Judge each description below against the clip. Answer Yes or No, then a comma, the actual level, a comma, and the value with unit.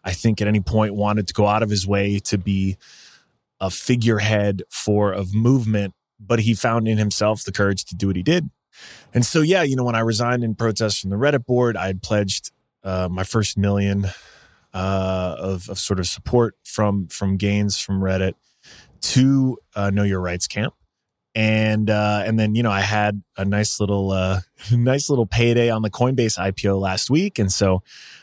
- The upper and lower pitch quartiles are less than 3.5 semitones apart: Yes, average, 2.7 semitones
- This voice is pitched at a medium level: No, low, 105 Hz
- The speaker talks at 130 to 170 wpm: No, average, 195 wpm